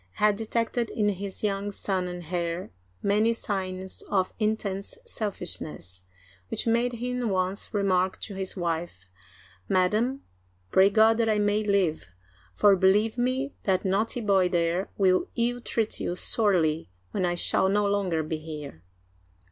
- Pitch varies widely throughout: No, average, 3.3 semitones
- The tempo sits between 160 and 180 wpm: No, average, 150 wpm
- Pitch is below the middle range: No, high, 195 Hz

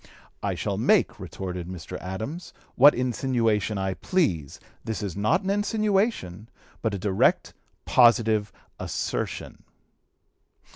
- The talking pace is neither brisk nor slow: No, slow, 110 wpm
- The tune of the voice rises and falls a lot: Yes, wide, 6.5 semitones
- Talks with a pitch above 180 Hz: No, low, 110 Hz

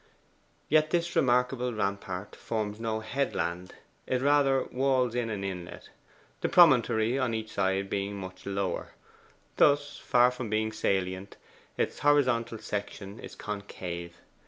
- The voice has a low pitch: Yes, low, 110 Hz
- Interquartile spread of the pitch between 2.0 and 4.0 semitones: No, average, 4.6 semitones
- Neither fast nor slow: No, slow, 130 wpm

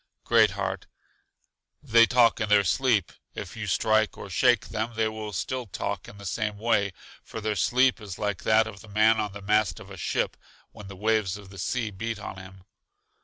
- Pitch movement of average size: No, narrow, 2.1 semitones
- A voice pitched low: Yes, low, 105 Hz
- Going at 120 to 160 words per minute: No, fast, 205 wpm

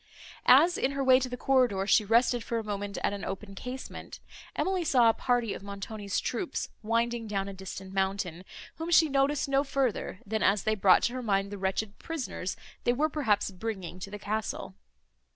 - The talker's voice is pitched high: Yes, high, 220 Hz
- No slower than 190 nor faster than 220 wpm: Yes, average, 195 wpm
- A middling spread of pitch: Yes, average, 4.6 semitones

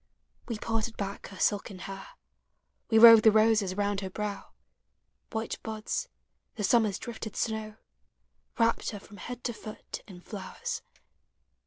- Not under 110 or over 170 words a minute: Yes, average, 150 wpm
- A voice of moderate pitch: No, high, 215 Hz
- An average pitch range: No, narrow, 2.0 semitones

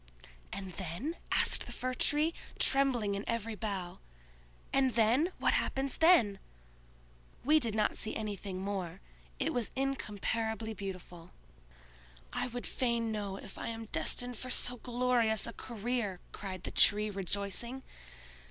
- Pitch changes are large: No, average, 3.8 semitones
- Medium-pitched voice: No, high, 220 Hz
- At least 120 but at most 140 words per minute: Yes, slow, 135 wpm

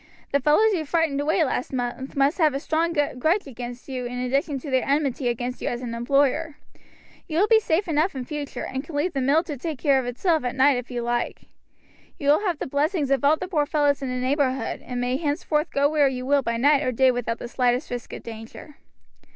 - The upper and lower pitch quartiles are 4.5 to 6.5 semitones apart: No, average, 3.4 semitones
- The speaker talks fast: Yes, fast, 235 wpm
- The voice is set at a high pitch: Yes, very high, 280 Hz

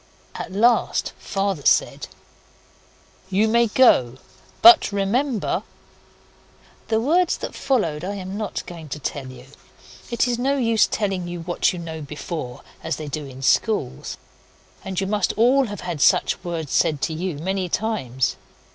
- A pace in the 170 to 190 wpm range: No, average, 155 wpm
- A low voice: No, high, 190 Hz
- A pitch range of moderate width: No, wide, 6.1 semitones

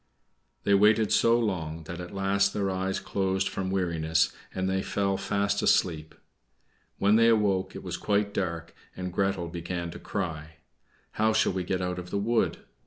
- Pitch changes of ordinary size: No, narrow, 2.3 semitones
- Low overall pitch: Yes, very low, 95 Hz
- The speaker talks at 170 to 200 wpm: Yes, average, 175 wpm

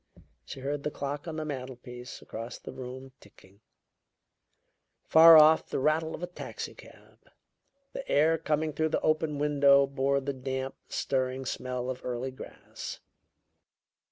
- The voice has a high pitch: No, medium, 140 Hz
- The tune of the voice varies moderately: Yes, average, 3.0 semitones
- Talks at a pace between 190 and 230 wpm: No, average, 140 wpm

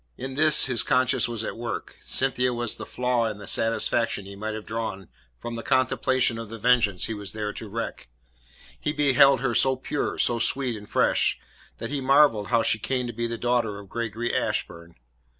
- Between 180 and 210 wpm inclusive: Yes, average, 200 wpm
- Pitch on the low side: Yes, low, 115 Hz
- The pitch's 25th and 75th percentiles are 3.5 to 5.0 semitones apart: No, average, 2.8 semitones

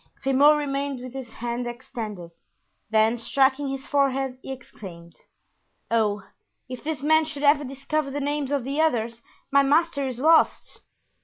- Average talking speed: Yes, average, 150 wpm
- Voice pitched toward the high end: Yes, very high, 270 Hz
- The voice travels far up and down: No, average, 3.2 semitones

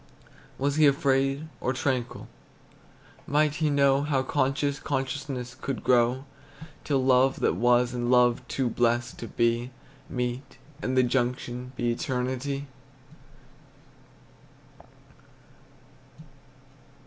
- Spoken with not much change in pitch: Yes, narrow, 2.1 semitones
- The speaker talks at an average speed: No, slow, 100 wpm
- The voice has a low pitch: Yes, low, 130 Hz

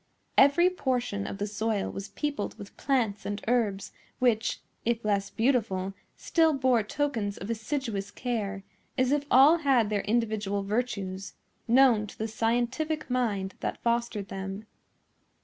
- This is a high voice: Yes, high, 225 Hz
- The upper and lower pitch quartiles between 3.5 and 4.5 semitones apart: Yes, average, 4.1 semitones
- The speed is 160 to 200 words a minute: No, average, 140 wpm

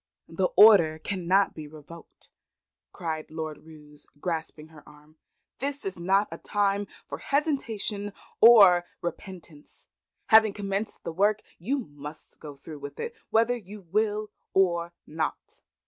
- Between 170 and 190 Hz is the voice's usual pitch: Yes, medium, 185 Hz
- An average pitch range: Yes, average, 4.9 semitones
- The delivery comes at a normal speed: No, slow, 130 wpm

